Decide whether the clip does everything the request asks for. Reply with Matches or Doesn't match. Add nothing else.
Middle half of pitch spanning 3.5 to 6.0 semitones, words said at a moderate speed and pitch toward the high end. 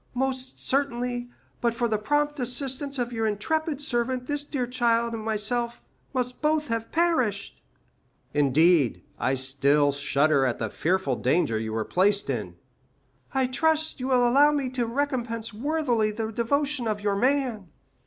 Matches